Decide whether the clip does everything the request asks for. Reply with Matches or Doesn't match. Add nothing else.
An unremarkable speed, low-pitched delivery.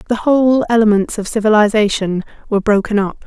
Doesn't match